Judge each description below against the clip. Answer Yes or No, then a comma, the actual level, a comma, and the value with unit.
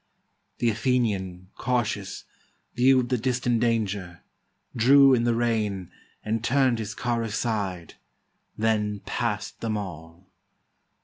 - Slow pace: Yes, slow, 110 wpm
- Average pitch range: Yes, average, 3.2 semitones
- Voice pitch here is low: Yes, low, 115 Hz